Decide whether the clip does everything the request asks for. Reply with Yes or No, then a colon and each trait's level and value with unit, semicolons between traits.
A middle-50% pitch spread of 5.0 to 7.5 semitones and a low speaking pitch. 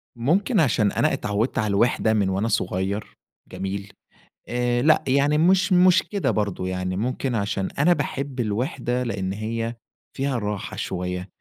Yes: wide, 5.4 semitones; low, 115 Hz